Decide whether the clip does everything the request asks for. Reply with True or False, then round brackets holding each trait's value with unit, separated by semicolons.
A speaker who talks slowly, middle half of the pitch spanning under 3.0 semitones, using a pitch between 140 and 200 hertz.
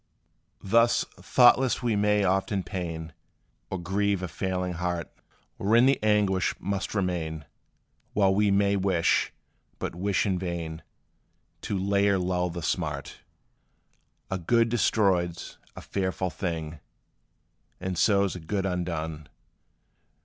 False (125 wpm; 2.6 semitones; 95 Hz)